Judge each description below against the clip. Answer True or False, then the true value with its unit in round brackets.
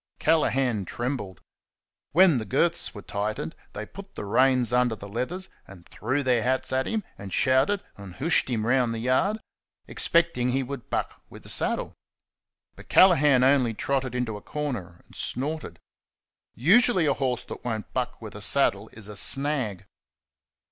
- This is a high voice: False (125 Hz)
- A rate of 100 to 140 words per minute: False (160 wpm)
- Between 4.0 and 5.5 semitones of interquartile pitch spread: True (4.7 semitones)